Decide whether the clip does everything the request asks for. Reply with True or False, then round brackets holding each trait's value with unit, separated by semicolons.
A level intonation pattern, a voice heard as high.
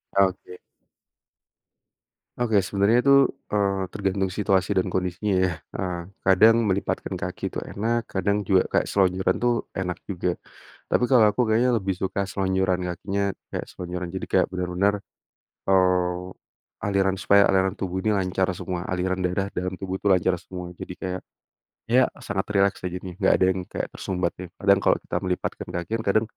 False (1.5 semitones; 95 Hz)